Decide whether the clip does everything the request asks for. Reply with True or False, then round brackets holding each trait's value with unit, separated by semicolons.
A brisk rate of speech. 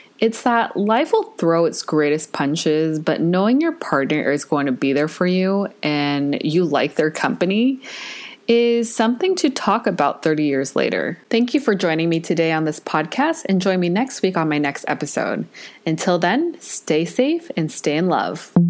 False (185 wpm)